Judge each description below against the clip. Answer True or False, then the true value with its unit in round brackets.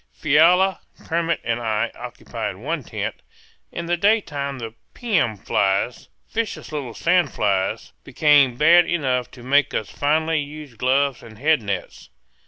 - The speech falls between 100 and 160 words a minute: True (140 wpm)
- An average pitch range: False (5.7 semitones)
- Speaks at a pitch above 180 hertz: False (140 Hz)